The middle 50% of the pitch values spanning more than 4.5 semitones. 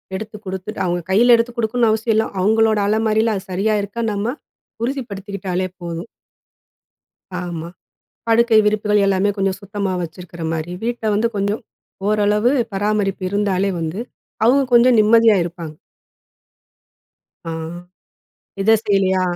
No: average, 2.8 semitones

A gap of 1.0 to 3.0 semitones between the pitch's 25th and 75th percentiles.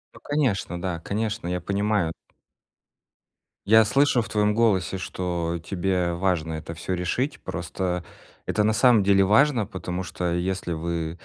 No: average, 3.5 semitones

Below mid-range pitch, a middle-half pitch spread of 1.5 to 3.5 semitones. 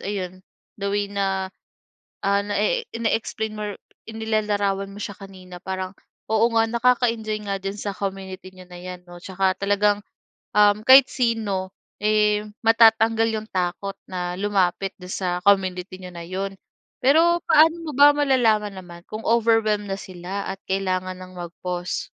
No: high, 200 Hz; average, 2.8 semitones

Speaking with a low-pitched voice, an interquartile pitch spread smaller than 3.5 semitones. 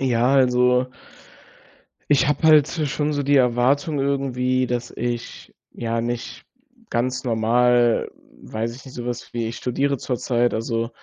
Yes: low, 125 Hz; narrow, 2.4 semitones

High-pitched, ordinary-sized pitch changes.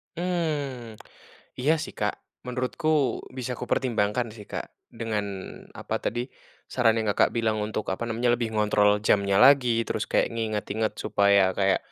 No: low, 115 Hz; average, 3.1 semitones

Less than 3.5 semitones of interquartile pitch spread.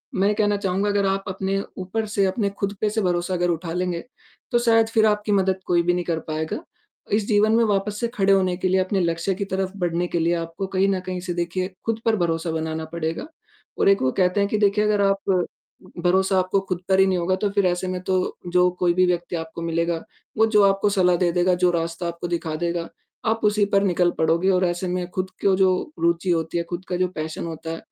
Yes: narrow, 2.4 semitones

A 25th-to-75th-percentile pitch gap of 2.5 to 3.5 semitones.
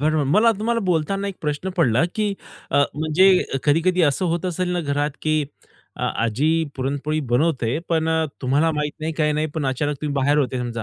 Yes: average, 3.1 semitones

